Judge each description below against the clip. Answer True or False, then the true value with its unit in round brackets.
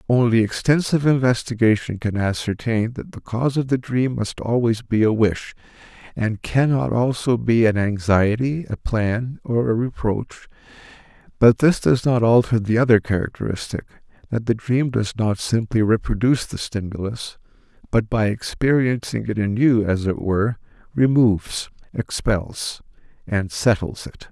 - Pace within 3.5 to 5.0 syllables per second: True (4.7 syllables/s)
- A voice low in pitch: True (115 Hz)